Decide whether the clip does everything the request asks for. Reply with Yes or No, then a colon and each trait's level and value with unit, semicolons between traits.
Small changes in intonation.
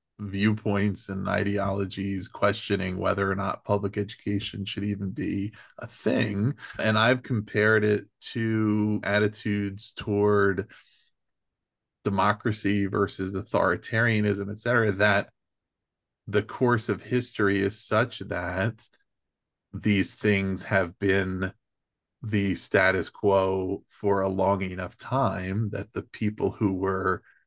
Yes: narrow, 1.6 semitones